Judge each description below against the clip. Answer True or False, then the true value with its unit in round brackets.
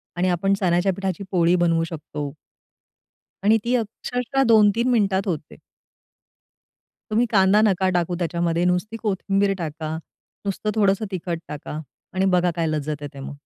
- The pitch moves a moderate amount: True (3.5 semitones)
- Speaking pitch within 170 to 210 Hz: True (185 Hz)